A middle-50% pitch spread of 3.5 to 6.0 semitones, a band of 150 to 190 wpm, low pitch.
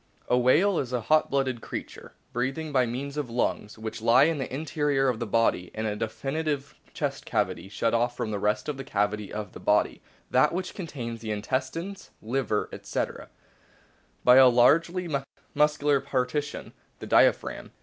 Yes: average, 4.4 semitones; average, 170 wpm; low, 130 Hz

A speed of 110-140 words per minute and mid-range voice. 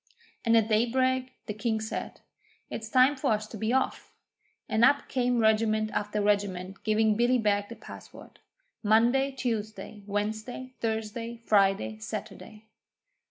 No: slow, 135 wpm; high, 220 Hz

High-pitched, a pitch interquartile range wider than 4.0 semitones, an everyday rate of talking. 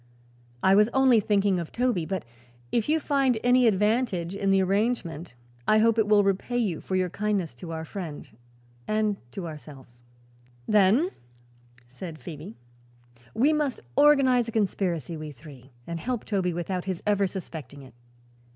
Yes: high, 195 Hz; average, 5.3 semitones; average, 160 wpm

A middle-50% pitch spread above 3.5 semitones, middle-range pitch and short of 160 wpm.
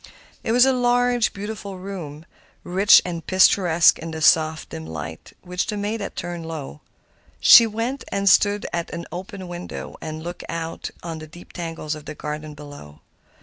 No: average, 4.3 semitones; medium, 175 Hz; average, 175 wpm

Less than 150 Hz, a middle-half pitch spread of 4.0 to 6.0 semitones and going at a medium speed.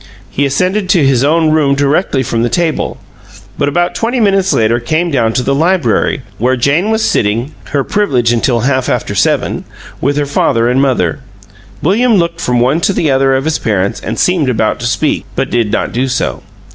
Yes: medium, 140 Hz; wide, 5.6 semitones; average, 195 wpm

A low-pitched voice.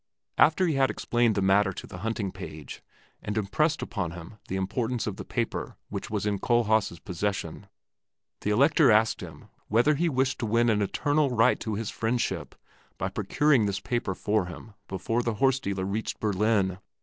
Yes: low, 110 Hz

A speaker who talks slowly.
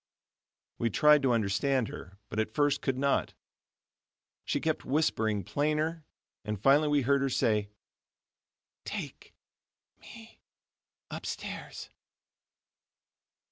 Yes: slow, 100 wpm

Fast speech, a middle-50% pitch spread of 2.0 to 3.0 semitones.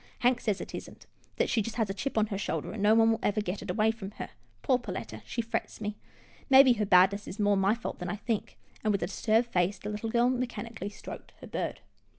Yes: fast, 245 wpm; narrow, 2.6 semitones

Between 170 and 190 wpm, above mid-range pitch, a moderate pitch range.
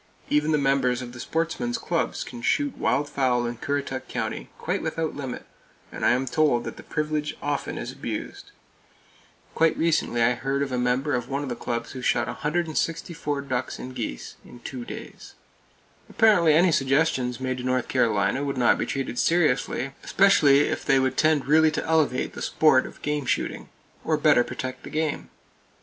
No: average, 180 wpm; medium, 140 Hz; average, 3.6 semitones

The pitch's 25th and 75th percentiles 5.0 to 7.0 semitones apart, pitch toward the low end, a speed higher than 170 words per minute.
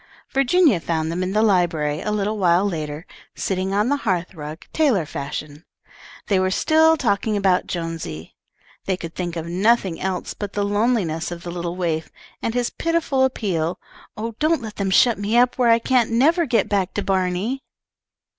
No: average, 5.3 semitones; high, 195 Hz; average, 180 wpm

